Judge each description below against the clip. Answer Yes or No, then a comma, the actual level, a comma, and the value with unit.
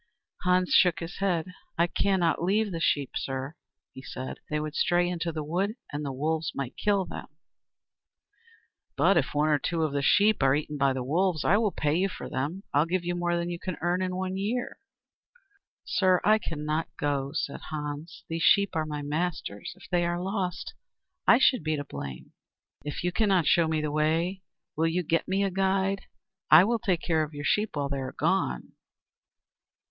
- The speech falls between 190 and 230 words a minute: Yes, average, 195 wpm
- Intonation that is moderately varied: Yes, average, 3.8 semitones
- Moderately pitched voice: Yes, medium, 170 Hz